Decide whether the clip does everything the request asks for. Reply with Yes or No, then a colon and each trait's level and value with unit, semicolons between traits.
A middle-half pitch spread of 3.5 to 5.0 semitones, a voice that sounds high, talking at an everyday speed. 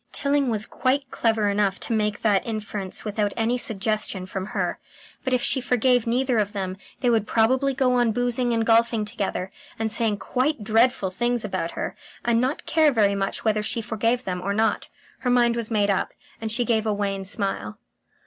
No: average, 3.0 semitones; high, 225 Hz; average, 195 wpm